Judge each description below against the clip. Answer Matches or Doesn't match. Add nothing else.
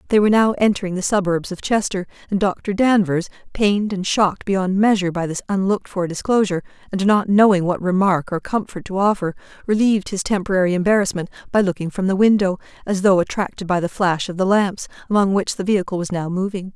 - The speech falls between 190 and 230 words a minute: Matches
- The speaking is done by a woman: Matches